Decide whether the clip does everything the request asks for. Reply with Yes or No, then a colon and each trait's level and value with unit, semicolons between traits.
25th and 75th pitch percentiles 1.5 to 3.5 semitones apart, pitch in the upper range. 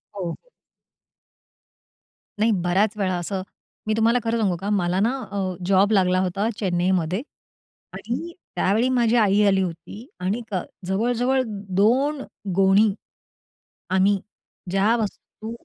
Yes: average, 3.2 semitones; high, 200 Hz